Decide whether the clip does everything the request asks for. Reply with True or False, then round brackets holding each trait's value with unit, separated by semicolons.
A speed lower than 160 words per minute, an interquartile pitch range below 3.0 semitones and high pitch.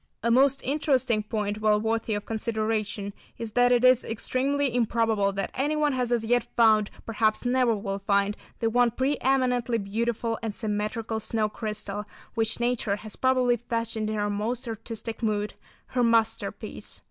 True (150 wpm; 2.5 semitones; 225 Hz)